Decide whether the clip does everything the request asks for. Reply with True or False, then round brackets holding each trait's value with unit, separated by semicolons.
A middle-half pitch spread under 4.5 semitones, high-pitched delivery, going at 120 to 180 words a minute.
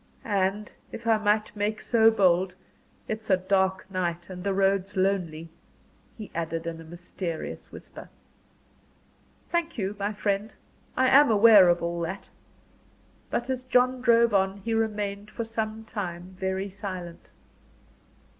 True (3.1 semitones; 200 Hz; 145 wpm)